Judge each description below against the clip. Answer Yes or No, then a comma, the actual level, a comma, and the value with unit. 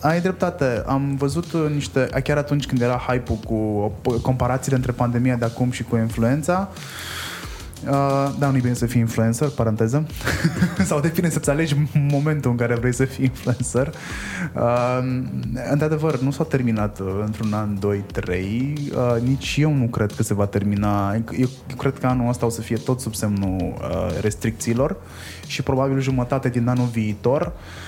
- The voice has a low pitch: Yes, low, 125 Hz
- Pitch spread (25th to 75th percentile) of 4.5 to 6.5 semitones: No, average, 4.0 semitones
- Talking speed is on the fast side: No, average, 155 wpm